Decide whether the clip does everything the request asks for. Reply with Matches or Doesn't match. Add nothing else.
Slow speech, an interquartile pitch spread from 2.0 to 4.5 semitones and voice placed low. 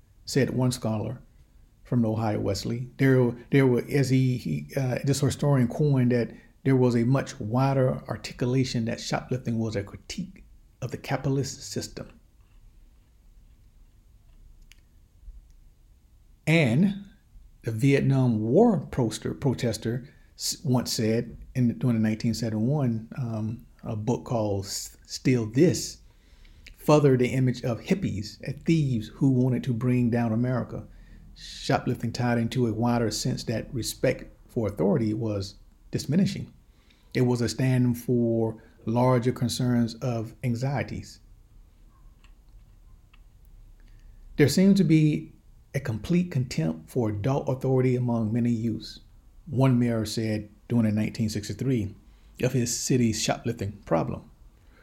Matches